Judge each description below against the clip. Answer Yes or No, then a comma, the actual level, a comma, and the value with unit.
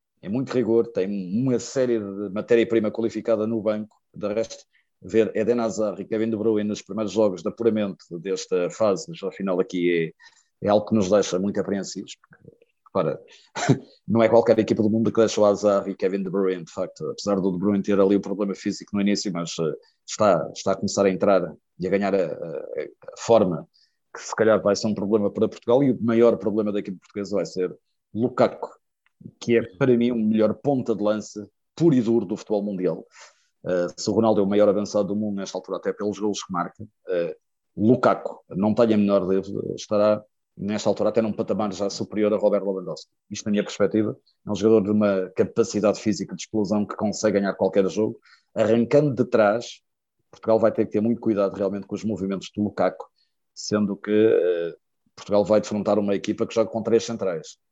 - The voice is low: Yes, low, 105 Hz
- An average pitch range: No, narrow, 2.1 semitones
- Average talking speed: No, fast, 205 wpm